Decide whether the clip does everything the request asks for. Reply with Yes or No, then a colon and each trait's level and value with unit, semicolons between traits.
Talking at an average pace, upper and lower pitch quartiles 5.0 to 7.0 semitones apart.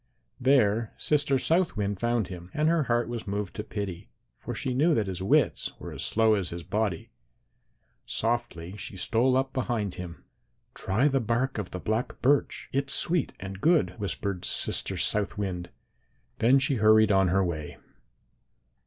Yes: average, 165 wpm; average, 5.3 semitones